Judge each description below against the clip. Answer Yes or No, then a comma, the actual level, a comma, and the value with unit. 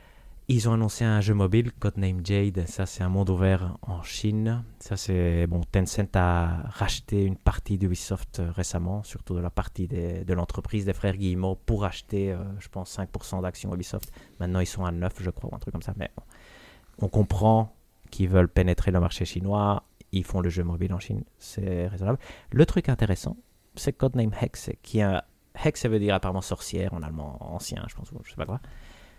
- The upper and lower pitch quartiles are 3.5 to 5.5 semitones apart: No, average, 3.0 semitones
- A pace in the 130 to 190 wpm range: No, average, 200 wpm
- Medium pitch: No, very low, 95 Hz